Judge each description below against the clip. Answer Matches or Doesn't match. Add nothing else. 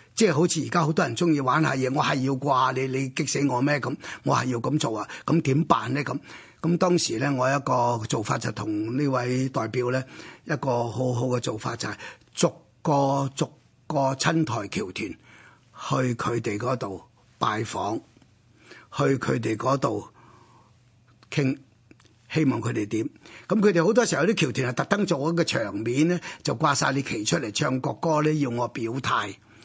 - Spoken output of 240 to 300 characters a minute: Matches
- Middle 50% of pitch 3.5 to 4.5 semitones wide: Matches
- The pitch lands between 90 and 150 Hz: Matches